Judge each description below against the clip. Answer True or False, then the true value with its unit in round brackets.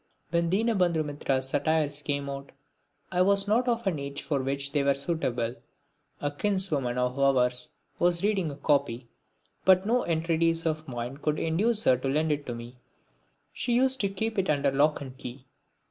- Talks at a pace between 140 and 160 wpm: False (175 wpm)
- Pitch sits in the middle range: True (150 Hz)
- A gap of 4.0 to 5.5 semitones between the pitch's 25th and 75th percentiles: True (5.2 semitones)